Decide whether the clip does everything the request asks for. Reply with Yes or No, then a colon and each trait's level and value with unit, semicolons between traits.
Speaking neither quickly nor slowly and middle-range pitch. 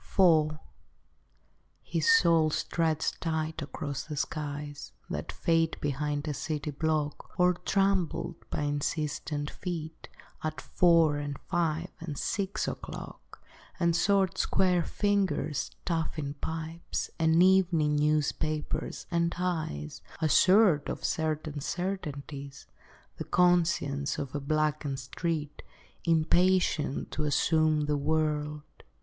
No: slow, 105 wpm; medium, 155 Hz